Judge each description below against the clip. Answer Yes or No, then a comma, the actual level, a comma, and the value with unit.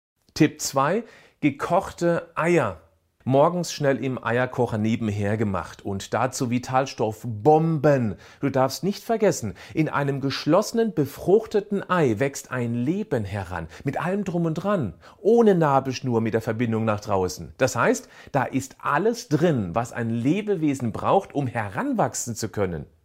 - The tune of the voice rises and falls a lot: Yes, wide, 6.7 semitones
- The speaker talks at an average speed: Yes, average, 135 wpm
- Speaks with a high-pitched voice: No, low, 130 Hz